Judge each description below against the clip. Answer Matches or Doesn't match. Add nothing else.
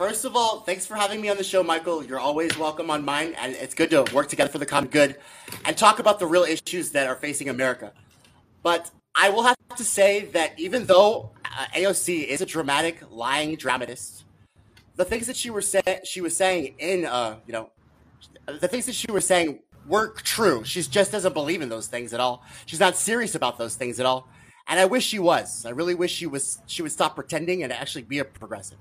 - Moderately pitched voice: Matches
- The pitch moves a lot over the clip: Matches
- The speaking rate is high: Matches